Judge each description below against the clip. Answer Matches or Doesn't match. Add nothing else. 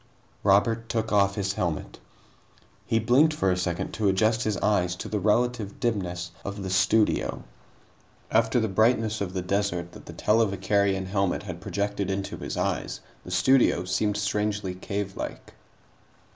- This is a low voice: Matches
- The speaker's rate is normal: Matches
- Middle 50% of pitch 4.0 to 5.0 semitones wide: Doesn't match